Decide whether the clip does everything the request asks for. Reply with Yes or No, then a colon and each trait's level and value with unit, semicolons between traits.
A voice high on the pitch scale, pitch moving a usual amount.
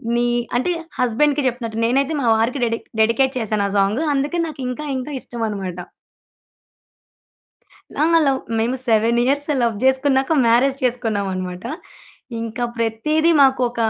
Yes: high, 245 Hz; average, 3.3 semitones